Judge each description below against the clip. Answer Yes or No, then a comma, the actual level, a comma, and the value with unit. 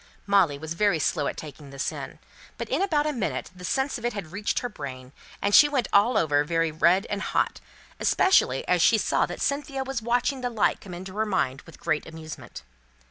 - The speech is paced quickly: Yes, fast, 215 wpm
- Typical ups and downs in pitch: No, wide, 7.6 semitones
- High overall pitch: Yes, high, 195 Hz